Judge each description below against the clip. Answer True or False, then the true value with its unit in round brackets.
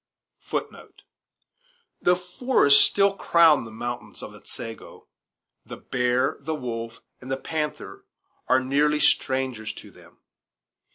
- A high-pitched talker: False (135 Hz)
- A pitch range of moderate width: True (4.2 semitones)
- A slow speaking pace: True (110 wpm)